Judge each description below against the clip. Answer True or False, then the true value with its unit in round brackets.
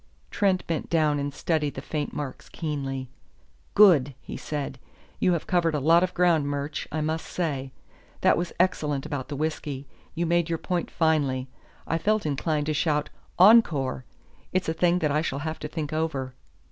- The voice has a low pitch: False (155 Hz)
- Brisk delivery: False (180 wpm)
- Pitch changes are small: False (3.0 semitones)